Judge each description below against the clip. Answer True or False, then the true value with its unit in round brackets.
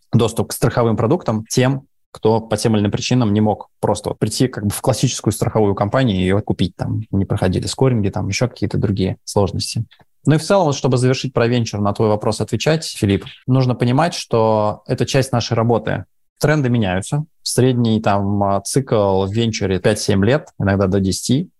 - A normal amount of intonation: True (3.9 semitones)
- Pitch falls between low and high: False (115 Hz)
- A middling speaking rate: False (185 wpm)